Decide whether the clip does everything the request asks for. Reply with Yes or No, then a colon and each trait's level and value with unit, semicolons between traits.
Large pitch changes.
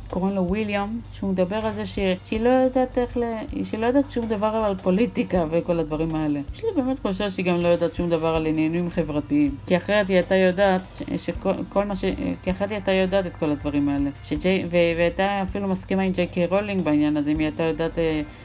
No: average, 3.8 semitones